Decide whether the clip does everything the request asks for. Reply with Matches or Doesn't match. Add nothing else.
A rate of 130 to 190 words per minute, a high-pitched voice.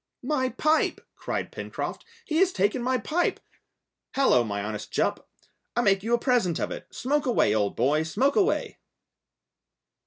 Matches